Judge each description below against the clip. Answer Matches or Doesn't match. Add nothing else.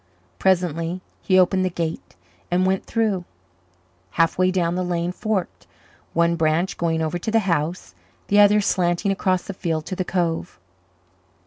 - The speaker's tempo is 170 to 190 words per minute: Doesn't match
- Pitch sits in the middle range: Matches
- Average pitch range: Doesn't match